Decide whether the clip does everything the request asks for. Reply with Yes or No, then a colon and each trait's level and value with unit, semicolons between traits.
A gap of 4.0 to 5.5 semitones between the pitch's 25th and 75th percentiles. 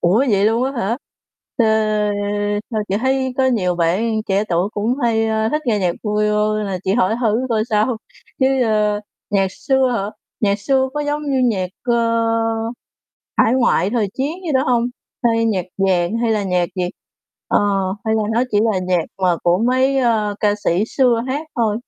No: average, 3.6 semitones